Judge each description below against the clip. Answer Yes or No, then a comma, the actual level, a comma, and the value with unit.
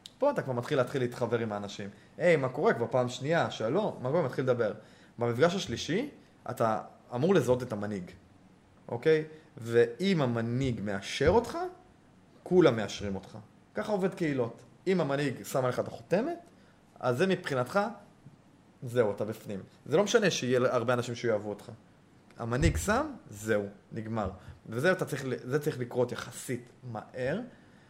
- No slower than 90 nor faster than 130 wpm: No, average, 145 wpm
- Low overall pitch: Yes, low, 125 Hz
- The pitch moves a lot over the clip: Yes, wide, 6.4 semitones